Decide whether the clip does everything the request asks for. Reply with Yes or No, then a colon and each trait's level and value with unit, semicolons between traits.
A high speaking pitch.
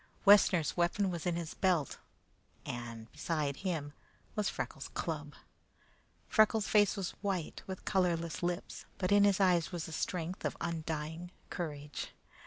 No: medium, 175 Hz